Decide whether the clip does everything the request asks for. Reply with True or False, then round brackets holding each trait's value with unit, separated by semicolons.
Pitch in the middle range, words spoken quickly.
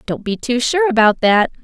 False (245 Hz; 220 wpm)